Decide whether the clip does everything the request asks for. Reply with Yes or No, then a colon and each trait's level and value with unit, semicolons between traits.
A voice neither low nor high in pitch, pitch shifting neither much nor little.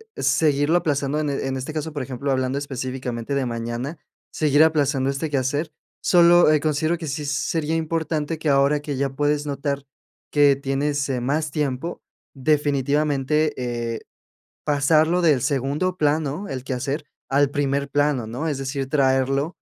No: medium, 145 Hz; narrow, 2.2 semitones